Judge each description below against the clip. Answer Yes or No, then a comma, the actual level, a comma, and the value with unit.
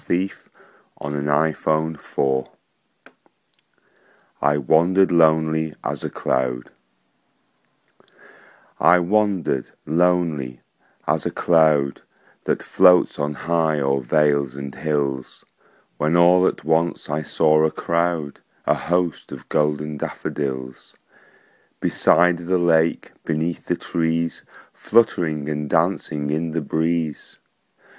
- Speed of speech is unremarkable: No, slow, 100 wpm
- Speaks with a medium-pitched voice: No, very low, 80 Hz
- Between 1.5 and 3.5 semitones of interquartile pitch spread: Yes, average, 2.7 semitones